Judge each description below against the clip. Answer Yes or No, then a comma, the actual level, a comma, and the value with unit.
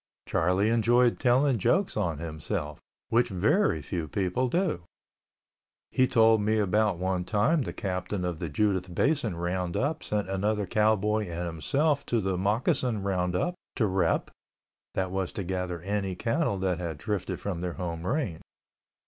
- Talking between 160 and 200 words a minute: No, average, 150 wpm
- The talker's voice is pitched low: Yes, very low, 95 Hz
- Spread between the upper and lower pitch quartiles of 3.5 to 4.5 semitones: Yes, average, 4.0 semitones